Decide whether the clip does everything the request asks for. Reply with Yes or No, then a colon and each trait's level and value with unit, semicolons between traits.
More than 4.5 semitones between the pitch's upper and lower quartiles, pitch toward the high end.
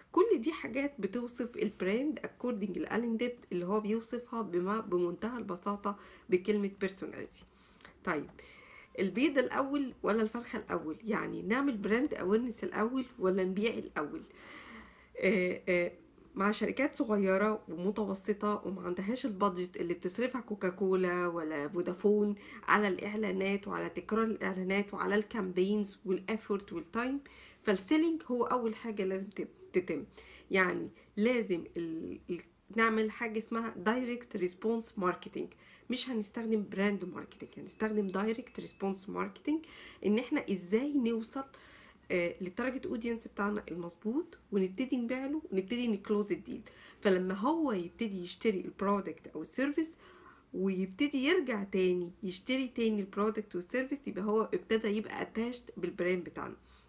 No: average, 4.2 semitones; high, 210 Hz